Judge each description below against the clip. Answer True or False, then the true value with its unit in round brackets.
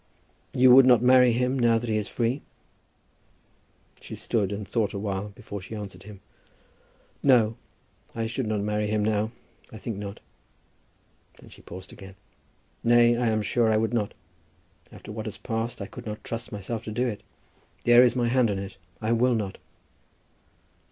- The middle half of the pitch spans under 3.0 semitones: True (2.5 semitones)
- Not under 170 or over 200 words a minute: True (180 wpm)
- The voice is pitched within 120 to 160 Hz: False (110 Hz)